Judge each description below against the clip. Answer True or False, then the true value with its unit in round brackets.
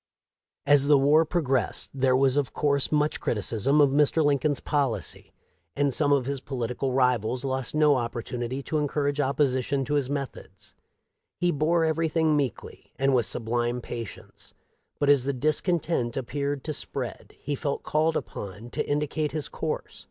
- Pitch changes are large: False (2.7 semitones)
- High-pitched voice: False (140 Hz)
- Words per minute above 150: True (165 wpm)